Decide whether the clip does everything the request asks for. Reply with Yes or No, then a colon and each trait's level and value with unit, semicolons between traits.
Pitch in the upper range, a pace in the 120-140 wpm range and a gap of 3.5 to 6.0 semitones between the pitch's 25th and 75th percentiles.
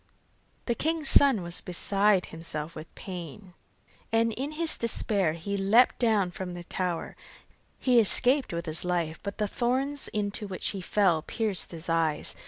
No: high, 195 Hz; average, 160 wpm; average, 5.2 semitones